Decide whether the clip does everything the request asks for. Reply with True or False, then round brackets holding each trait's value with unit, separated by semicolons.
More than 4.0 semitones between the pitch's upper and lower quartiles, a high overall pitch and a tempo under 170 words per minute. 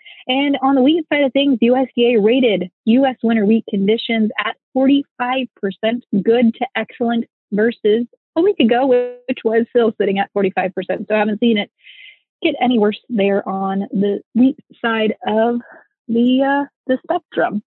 False (3.5 semitones; 240 Hz; 160 wpm)